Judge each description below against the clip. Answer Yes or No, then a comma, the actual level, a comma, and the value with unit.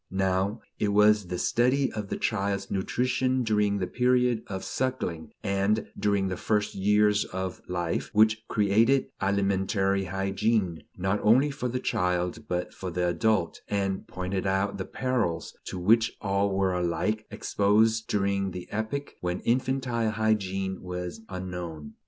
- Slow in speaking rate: No, average, 145 wpm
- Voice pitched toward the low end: Yes, low, 100 Hz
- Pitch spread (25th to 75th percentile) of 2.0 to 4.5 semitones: Yes, average, 2.8 semitones